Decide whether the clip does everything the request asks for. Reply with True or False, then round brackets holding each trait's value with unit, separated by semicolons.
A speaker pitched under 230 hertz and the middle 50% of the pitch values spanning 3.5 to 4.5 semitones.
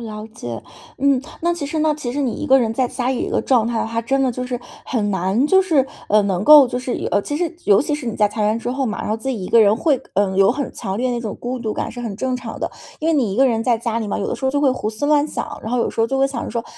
False (240 Hz; 3.8 semitones)